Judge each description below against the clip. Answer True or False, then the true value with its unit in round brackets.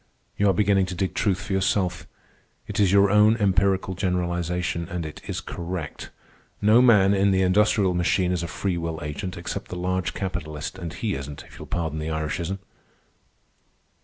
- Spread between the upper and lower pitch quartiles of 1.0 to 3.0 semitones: True (2.4 semitones)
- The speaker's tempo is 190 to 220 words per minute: False (175 wpm)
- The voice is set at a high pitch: False (90 Hz)